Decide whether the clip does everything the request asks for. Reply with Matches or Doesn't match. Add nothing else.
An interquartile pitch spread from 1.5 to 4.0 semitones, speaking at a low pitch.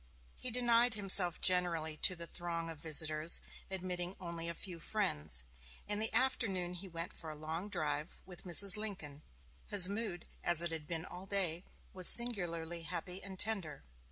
Doesn't match